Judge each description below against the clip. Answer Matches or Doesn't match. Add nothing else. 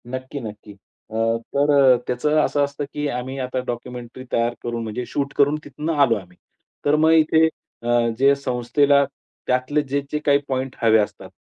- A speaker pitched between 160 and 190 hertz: Doesn't match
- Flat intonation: Doesn't match